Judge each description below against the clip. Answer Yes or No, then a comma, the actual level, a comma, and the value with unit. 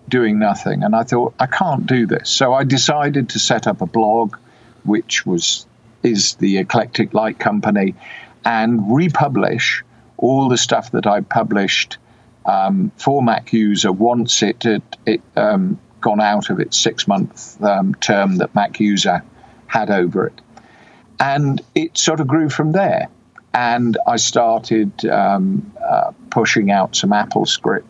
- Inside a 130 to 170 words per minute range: Yes, average, 155 wpm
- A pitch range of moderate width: No, wide, 6.4 semitones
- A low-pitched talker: Yes, low, 120 Hz